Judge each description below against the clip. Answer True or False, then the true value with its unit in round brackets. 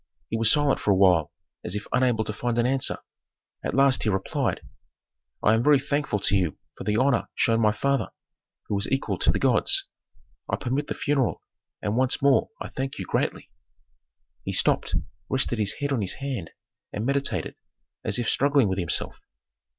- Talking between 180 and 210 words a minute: True (185 wpm)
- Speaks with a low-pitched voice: True (120 Hz)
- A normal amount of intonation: True (4.7 semitones)